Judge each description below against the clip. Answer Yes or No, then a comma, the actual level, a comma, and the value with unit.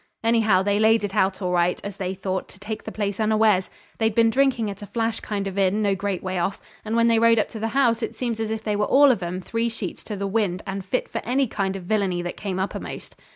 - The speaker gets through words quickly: Yes, fast, 260 wpm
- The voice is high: Yes, high, 210 Hz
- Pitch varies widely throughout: No, average, 2.9 semitones